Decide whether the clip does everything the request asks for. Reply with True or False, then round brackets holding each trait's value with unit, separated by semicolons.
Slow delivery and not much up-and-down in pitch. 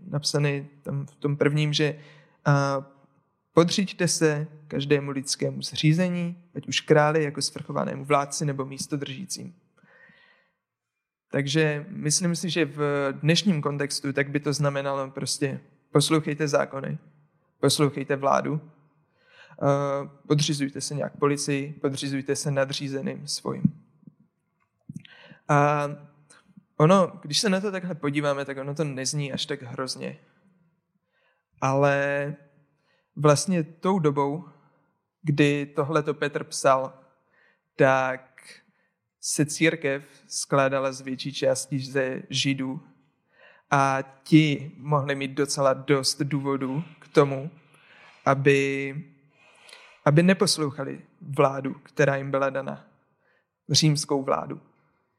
True (100 wpm; 2.0 semitones)